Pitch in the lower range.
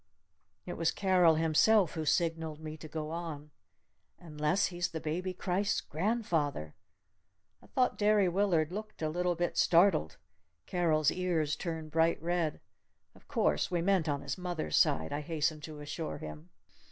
No: medium, 165 Hz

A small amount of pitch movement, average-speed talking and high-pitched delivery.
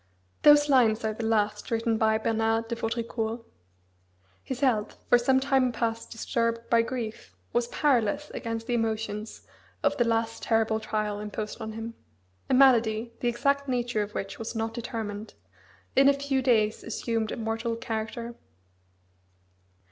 Yes: narrow, 1.7 semitones; average, 150 wpm; high, 230 Hz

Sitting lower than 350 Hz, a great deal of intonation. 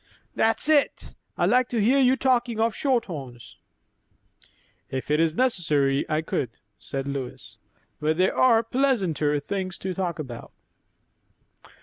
Yes: medium, 185 Hz; wide, 8.5 semitones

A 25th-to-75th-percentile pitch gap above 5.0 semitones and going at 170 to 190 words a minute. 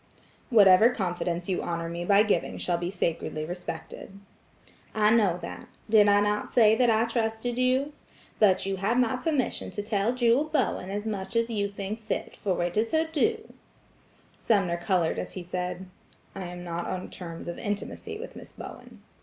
No: average, 4.3 semitones; average, 180 wpm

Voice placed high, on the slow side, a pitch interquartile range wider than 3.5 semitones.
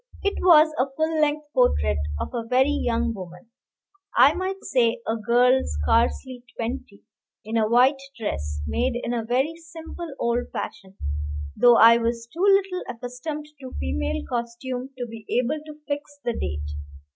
No: high, 245 Hz; average, 155 wpm; average, 4.5 semitones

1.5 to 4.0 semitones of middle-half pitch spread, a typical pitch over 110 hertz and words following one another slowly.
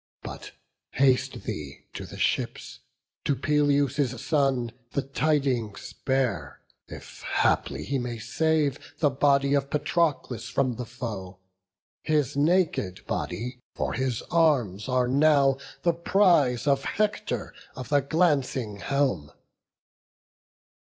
Yes: average, 3.4 semitones; low, 135 Hz; slow, 115 wpm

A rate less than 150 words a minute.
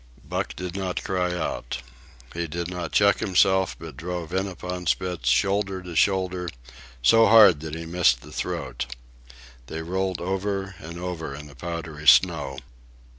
No: average, 155 wpm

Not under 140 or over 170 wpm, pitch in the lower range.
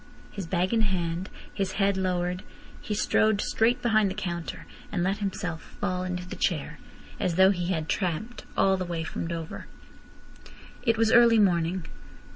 No: average, 165 wpm; medium, 185 Hz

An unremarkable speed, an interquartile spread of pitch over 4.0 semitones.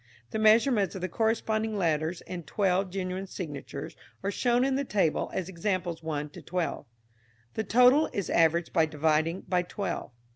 Yes: average, 160 wpm; average, 4.7 semitones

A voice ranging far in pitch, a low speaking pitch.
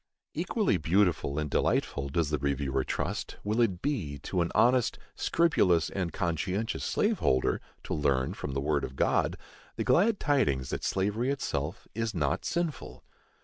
Yes: wide, 8.4 semitones; very low, 85 Hz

